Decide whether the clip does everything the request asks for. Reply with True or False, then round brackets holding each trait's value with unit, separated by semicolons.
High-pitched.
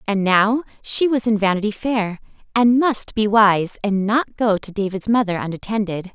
True (210 Hz)